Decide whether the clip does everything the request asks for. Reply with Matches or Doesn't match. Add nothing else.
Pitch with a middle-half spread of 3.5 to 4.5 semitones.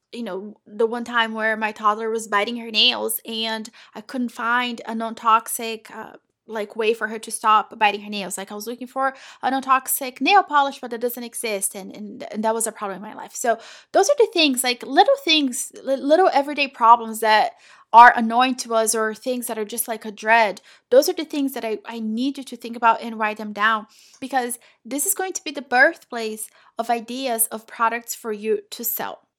Doesn't match